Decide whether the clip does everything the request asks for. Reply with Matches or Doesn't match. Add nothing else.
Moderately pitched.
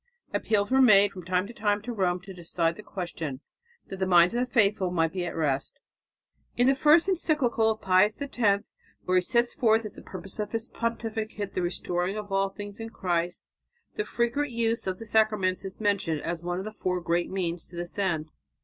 Doesn't match